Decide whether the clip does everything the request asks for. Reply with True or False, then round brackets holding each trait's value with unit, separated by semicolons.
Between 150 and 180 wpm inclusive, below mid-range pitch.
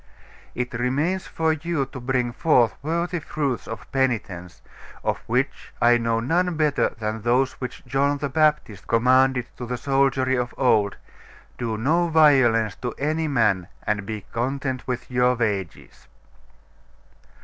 False (140 wpm; 125 Hz)